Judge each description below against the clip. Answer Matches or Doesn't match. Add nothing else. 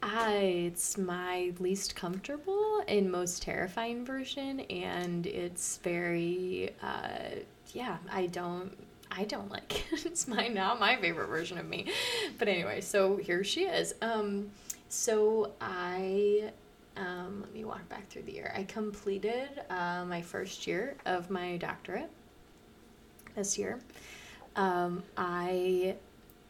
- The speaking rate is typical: Doesn't match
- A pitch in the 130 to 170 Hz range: Doesn't match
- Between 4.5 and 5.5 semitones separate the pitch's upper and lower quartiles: Doesn't match